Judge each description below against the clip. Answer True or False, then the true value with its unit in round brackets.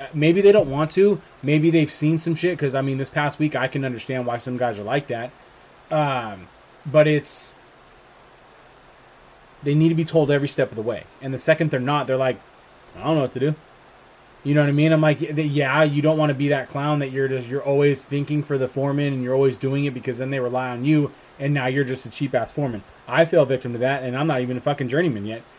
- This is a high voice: False (140 Hz)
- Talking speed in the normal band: False (250 wpm)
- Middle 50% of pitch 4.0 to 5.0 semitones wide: False (2.7 semitones)